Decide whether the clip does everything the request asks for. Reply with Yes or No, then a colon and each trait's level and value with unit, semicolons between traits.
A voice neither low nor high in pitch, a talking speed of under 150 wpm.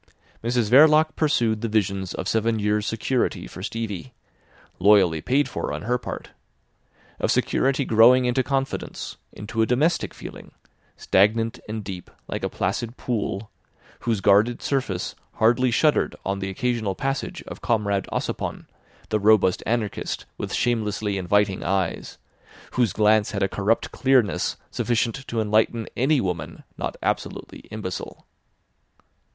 No: low, 110 Hz; slow, 135 wpm